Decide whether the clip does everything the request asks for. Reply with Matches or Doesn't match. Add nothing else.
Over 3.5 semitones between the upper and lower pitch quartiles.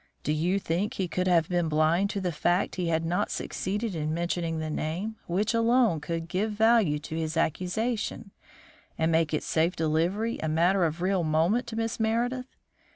Matches